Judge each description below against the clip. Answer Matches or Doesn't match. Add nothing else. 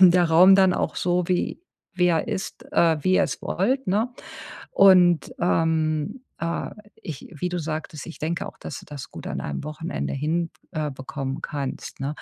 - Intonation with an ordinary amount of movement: Matches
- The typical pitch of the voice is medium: Matches